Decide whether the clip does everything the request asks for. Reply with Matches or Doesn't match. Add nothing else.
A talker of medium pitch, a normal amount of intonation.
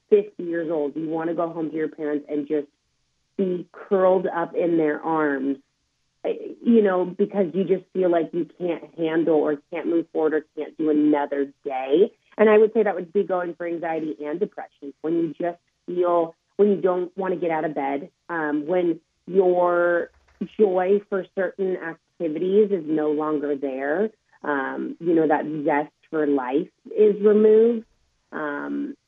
Matches